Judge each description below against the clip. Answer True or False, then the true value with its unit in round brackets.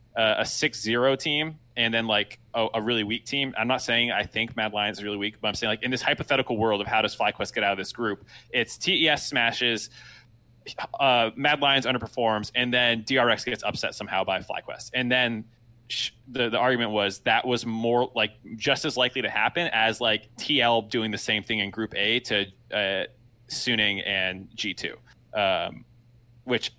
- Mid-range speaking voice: False (115 Hz)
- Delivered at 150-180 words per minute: False (195 wpm)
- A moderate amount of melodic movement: False (2.3 semitones)